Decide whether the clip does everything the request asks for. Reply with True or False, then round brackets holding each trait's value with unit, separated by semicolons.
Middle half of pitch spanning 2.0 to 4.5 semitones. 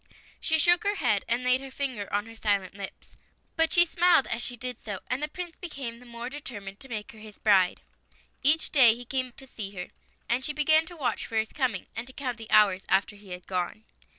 False (5.2 semitones)